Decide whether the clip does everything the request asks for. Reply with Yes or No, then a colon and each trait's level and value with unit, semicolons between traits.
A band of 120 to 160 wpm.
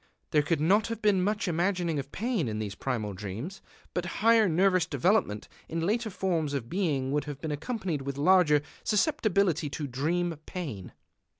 No: average, 170 wpm